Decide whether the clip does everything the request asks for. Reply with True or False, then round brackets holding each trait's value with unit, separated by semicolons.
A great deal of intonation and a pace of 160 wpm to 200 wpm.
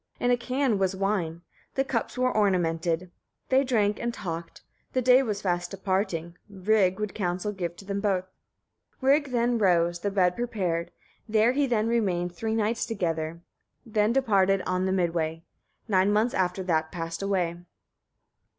False (4.2 semitones; 165 wpm)